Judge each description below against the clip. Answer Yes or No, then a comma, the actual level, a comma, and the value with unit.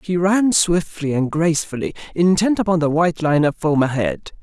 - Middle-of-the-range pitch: Yes, medium, 165 Hz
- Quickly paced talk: No, average, 175 wpm